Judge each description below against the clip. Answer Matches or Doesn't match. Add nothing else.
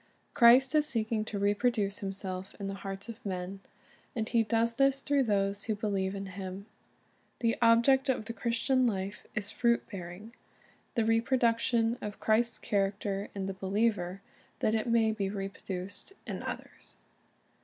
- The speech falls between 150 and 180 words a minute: Matches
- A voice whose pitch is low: Doesn't match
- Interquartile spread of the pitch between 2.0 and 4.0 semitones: Matches